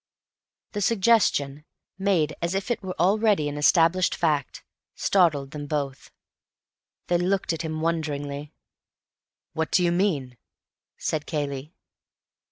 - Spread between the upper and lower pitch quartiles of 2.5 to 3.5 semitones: No, average, 4.1 semitones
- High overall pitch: No, medium, 160 Hz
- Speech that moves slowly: Yes, slow, 120 wpm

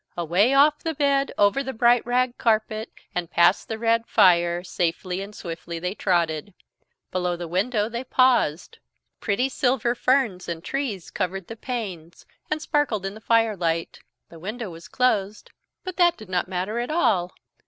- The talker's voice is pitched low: No, high, 210 Hz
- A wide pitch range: Yes, wide, 5.8 semitones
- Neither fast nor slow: Yes, average, 165 wpm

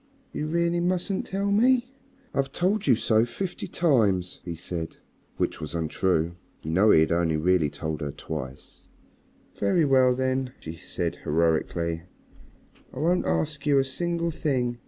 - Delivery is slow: No, average, 155 wpm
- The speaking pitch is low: Yes, low, 125 Hz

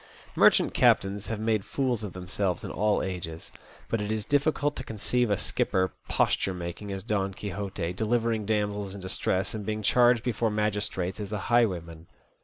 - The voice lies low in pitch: Yes, low, 105 Hz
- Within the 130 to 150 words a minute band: No, average, 170 wpm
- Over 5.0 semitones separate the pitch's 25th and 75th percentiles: No, average, 2.8 semitones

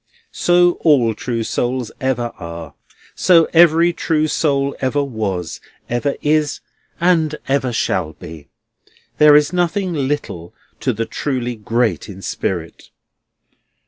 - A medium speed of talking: No, slow, 120 wpm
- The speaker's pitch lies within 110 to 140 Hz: Yes, low, 135 Hz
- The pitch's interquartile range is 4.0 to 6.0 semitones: Yes, wide, 5.6 semitones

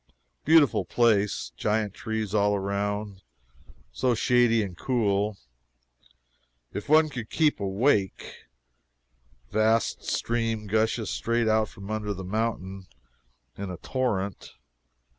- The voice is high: No, low, 110 Hz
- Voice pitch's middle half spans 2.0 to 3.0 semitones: Yes, narrow, 2.6 semitones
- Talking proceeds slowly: Yes, slow, 105 wpm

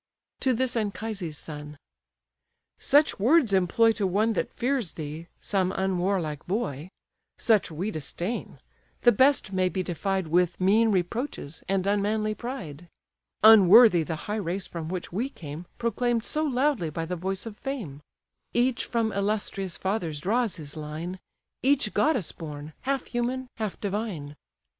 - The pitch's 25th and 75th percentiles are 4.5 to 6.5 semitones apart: Yes, average, 5.2 semitones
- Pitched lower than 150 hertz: No, high, 195 Hz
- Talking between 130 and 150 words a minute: Yes, average, 145 wpm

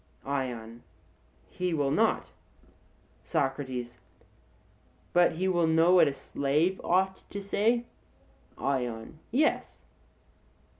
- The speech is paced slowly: Yes, slow, 95 wpm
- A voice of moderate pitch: Yes, medium, 160 Hz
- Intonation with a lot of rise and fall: Yes, wide, 5.9 semitones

